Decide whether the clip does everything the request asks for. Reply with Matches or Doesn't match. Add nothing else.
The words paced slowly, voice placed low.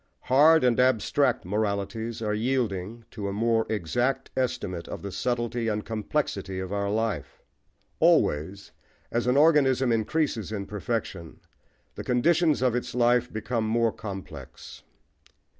Matches